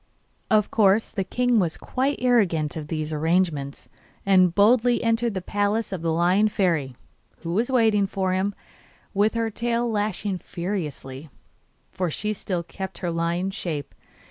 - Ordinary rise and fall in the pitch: Yes, average, 4.4 semitones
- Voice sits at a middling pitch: No, high, 195 Hz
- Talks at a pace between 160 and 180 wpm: No, average, 150 wpm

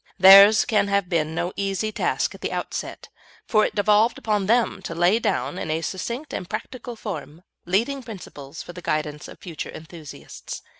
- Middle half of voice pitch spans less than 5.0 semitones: Yes, average, 4.4 semitones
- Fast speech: No, average, 180 wpm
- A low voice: No, high, 195 Hz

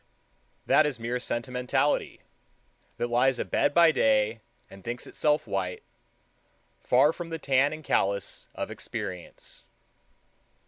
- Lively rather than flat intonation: No, average, 4.9 semitones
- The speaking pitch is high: No, low, 125 Hz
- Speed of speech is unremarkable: No, slow, 120 wpm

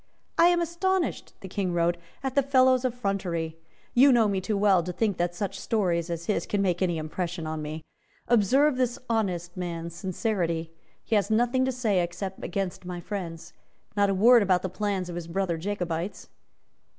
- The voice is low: No, high, 190 Hz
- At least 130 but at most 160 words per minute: No, average, 185 wpm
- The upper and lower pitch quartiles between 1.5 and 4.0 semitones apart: No, average, 4.6 semitones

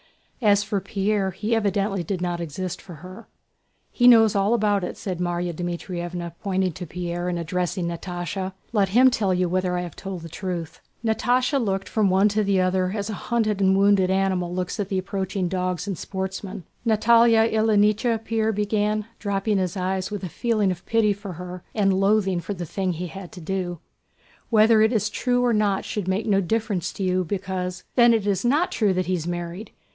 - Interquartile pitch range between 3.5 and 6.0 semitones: No, average, 2.8 semitones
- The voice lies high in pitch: Yes, high, 195 Hz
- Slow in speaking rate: No, average, 195 wpm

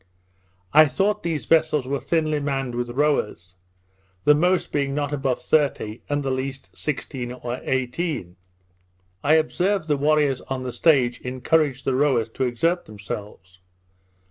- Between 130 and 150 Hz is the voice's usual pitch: Yes, medium, 140 Hz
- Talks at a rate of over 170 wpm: No, average, 145 wpm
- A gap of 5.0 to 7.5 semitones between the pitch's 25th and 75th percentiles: No, average, 3.5 semitones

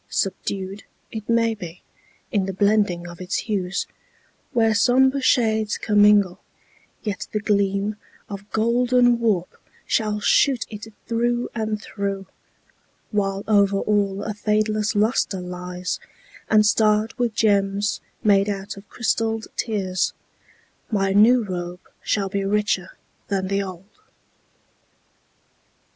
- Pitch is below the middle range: No, high, 205 Hz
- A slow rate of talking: Yes, slow, 120 wpm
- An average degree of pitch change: No, narrow, 2.1 semitones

